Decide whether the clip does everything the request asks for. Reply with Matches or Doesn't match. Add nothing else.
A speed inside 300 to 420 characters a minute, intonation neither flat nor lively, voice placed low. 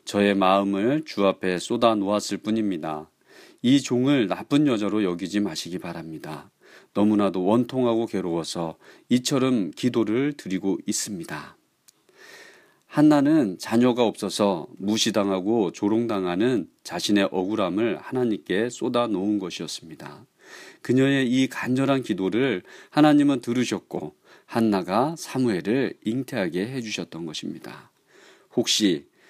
Doesn't match